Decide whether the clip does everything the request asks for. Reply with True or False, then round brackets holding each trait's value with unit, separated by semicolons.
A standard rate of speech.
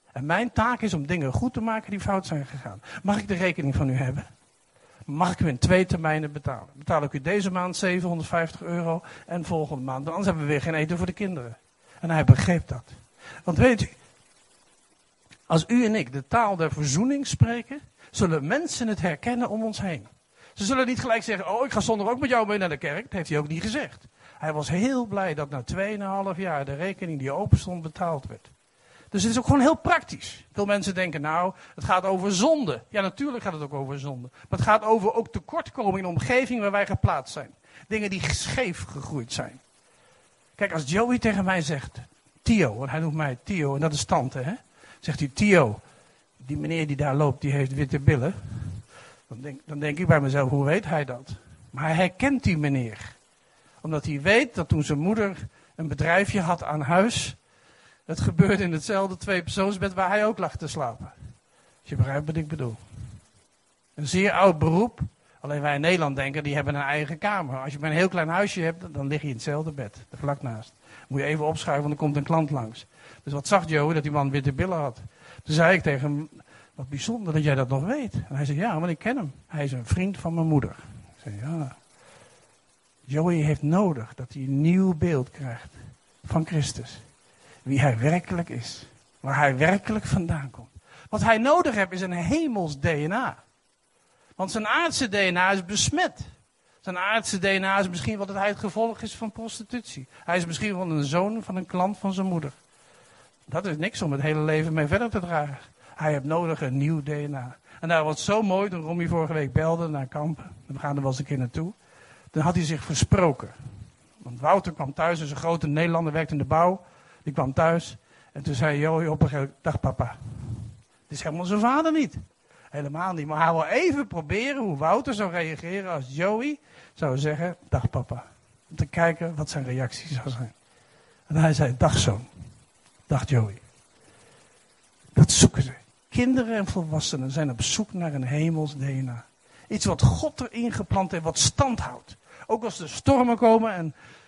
False (205 wpm)